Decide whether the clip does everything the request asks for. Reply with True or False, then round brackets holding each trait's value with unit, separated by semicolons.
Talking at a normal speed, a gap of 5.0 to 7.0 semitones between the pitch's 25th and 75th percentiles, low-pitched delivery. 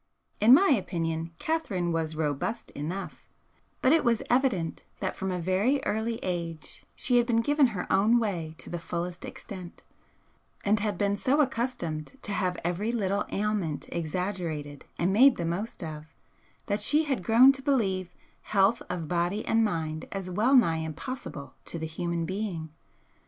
False (160 wpm; 5.4 semitones; 190 Hz)